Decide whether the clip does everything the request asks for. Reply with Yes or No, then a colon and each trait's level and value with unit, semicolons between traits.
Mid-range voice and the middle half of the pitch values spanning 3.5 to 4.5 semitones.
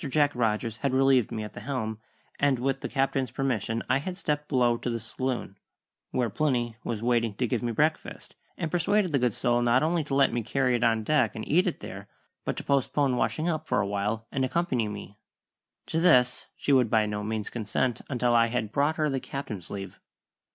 No: low, 125 Hz; average, 3.8 semitones